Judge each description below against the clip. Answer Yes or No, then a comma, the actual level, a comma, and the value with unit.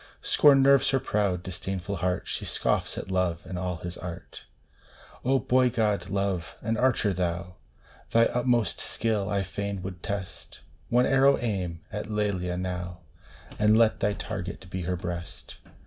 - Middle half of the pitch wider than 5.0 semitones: No, average, 3.8 semitones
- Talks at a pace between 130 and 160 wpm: Yes, average, 155 wpm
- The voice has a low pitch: Yes, low, 100 Hz